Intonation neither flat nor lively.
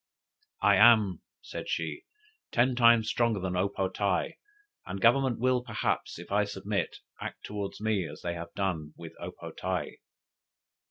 Yes: average, 4.2 semitones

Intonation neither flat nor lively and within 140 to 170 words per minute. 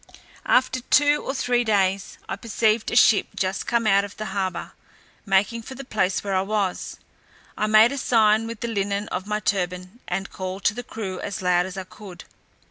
No: average, 3.1 semitones; average, 200 wpm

